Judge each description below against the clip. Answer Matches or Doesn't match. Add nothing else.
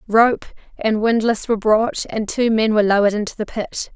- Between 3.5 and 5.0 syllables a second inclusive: Doesn't match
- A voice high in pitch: Matches